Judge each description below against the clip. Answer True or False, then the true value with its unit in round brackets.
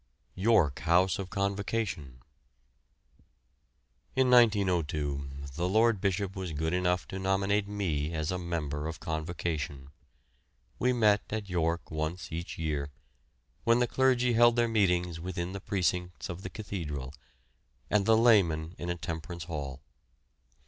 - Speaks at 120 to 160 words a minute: True (135 wpm)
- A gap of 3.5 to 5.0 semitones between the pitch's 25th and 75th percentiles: True (4.3 semitones)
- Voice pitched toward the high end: False (90 Hz)